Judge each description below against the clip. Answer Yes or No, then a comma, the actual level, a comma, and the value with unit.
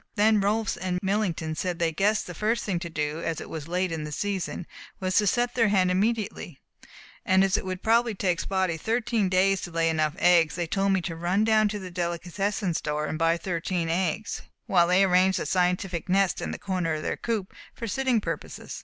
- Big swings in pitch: No, average, 3.3 semitones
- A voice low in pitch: No, medium, 185 Hz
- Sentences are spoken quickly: Yes, fast, 215 wpm